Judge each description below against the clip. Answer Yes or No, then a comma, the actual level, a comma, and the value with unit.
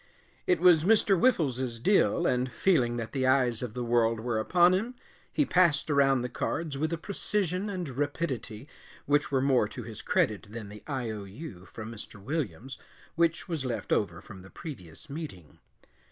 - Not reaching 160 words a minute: No, average, 180 wpm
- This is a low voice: Yes, low, 130 Hz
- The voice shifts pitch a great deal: Yes, wide, 6.6 semitones